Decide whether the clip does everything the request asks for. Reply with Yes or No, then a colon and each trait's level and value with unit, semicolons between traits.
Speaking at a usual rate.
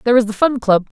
No: fast, 305 wpm